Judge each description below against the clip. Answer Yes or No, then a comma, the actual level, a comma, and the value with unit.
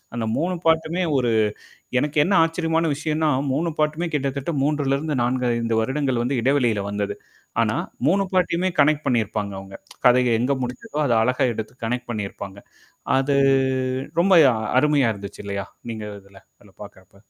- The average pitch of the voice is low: Yes, low, 130 Hz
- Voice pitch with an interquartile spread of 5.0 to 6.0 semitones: Yes, wide, 5.4 semitones